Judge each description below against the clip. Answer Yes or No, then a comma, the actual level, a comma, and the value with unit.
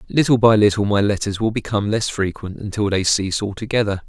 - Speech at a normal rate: Yes, average, 190 wpm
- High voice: No, low, 105 Hz